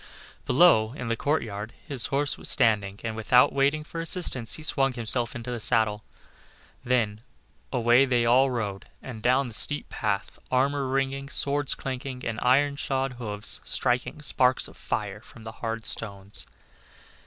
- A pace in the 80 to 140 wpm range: No, average, 155 wpm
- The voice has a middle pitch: No, low, 125 Hz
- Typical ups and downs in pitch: Yes, average, 3.5 semitones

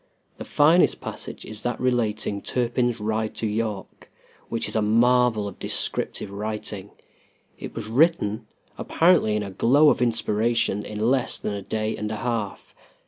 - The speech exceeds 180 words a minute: No, average, 155 wpm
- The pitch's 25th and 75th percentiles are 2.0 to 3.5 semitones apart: Yes, narrow, 2.5 semitones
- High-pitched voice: No, low, 110 Hz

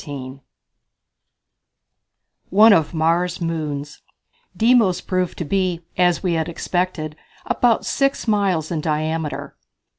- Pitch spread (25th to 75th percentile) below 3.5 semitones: Yes, average, 3.1 semitones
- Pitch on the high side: No, medium, 170 Hz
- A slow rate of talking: Yes, slow, 110 wpm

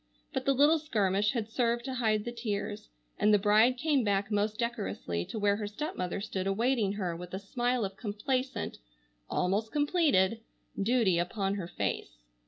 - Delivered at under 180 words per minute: Yes, average, 160 wpm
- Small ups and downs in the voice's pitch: No, average, 3.8 semitones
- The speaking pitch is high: Yes, high, 210 Hz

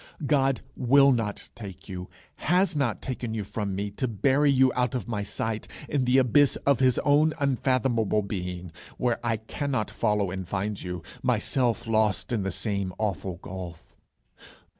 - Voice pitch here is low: Yes, low, 115 Hz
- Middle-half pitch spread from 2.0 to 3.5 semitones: No, average, 4.7 semitones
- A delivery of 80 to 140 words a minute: No, average, 160 wpm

